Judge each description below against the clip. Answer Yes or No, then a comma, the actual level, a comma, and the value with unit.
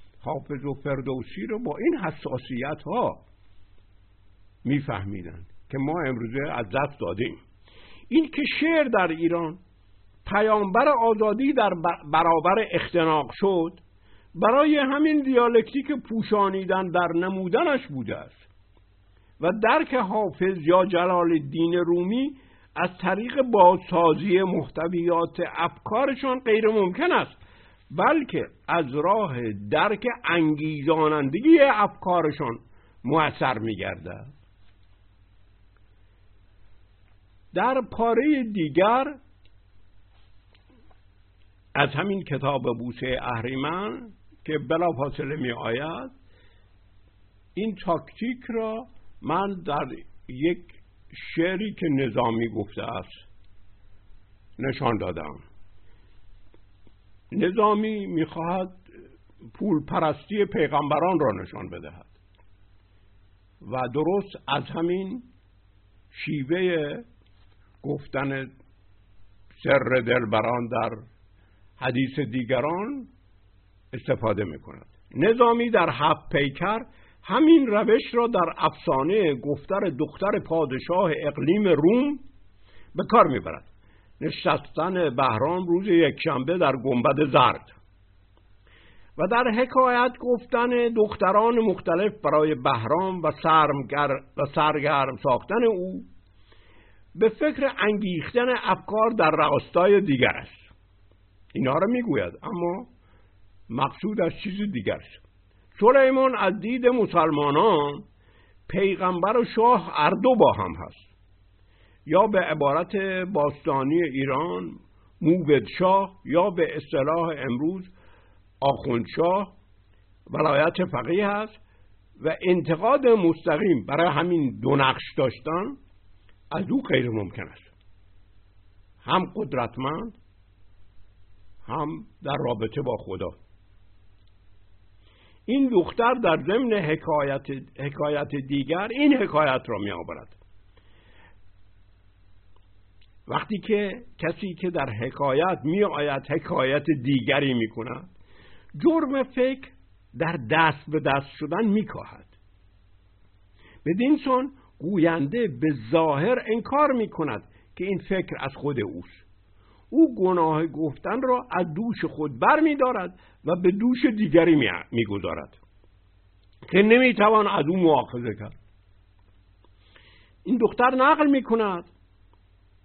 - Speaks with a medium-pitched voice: Yes, medium, 145 Hz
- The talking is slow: Yes, slow, 100 wpm